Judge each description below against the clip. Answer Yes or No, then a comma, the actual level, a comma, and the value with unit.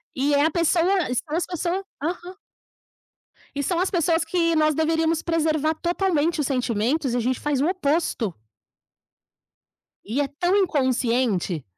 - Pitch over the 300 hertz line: Yes, very high, 310 Hz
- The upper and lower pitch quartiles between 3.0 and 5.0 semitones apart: Yes, average, 4.3 semitones